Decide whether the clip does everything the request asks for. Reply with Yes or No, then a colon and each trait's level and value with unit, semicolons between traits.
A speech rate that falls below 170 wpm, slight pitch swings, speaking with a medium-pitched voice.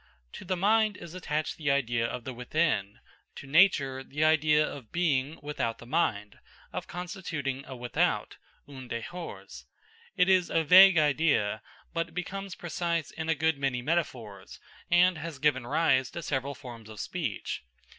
No: average, 155 wpm; average, 4.7 semitones; medium, 150 Hz